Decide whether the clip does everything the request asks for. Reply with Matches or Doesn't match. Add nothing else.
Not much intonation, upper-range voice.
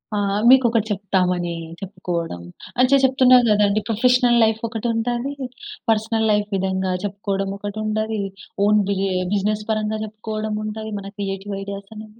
Matches